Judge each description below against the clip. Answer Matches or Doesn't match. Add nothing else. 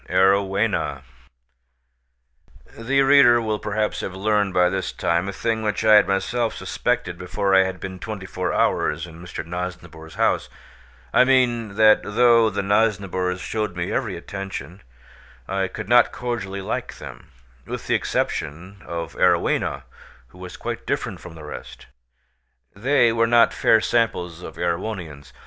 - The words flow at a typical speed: Matches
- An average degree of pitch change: Matches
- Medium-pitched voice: Doesn't match